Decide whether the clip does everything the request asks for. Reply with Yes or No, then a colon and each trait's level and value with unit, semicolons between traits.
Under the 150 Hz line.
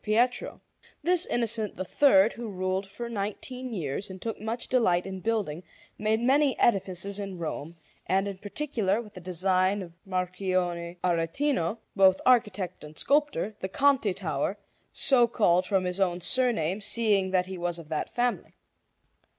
No: high, 195 Hz